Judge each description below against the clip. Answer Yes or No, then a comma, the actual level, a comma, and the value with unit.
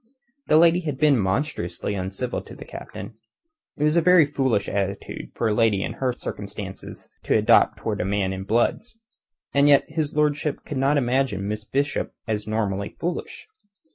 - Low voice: Yes, low, 125 Hz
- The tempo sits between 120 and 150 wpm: No, average, 170 wpm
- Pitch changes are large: Yes, wide, 6.7 semitones